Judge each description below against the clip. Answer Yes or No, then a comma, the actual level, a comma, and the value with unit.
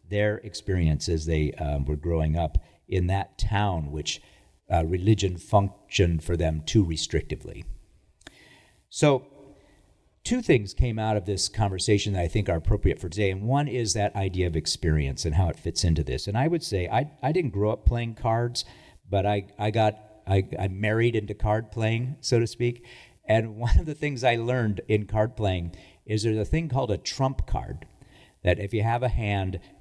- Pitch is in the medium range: No, low, 105 Hz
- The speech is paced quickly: No, average, 190 wpm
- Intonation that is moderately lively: Yes, average, 4.6 semitones